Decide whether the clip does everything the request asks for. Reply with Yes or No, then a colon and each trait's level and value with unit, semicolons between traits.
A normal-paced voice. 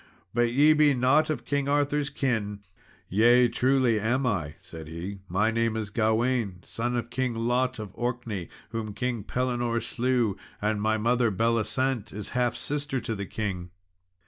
Yes: average, 160 wpm